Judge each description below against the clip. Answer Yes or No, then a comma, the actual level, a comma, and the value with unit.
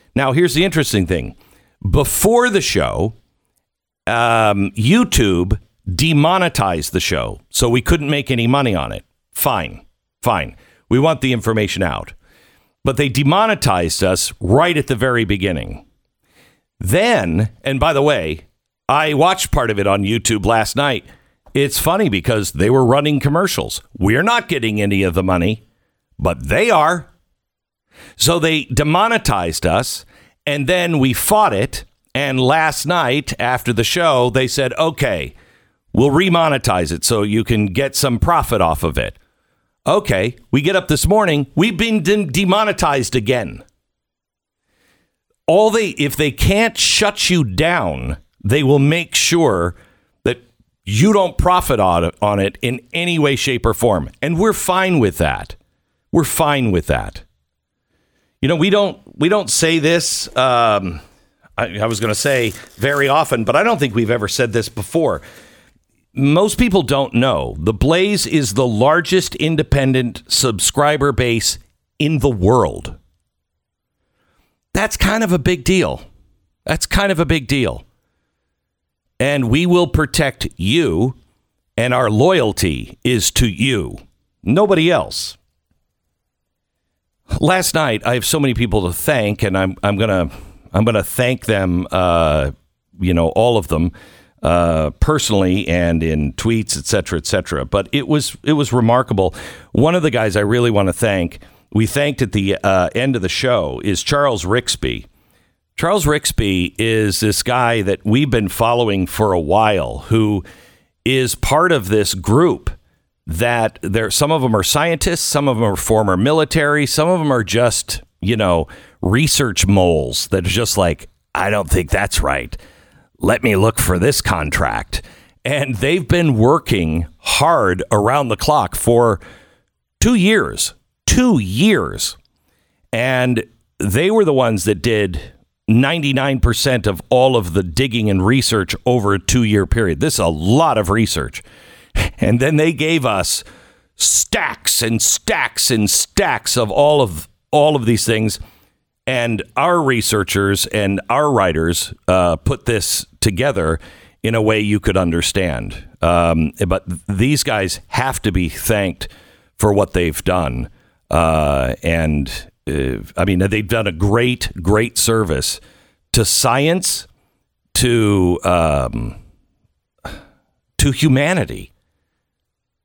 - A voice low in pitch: Yes, low, 115 Hz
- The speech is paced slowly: No, average, 145 wpm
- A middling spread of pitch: No, wide, 6.7 semitones